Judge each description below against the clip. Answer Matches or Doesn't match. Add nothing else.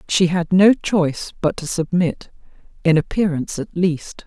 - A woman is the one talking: Matches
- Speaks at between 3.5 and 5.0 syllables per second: Matches